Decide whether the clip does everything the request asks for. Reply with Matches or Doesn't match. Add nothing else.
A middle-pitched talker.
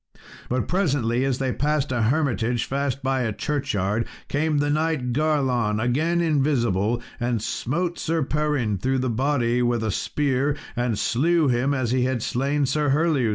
Doesn't match